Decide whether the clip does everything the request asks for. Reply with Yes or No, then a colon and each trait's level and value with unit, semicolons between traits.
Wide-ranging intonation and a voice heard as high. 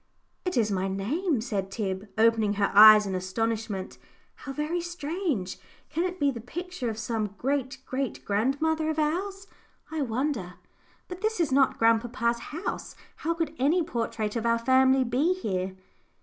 Yes: wide, 6.6 semitones; very high, 250 Hz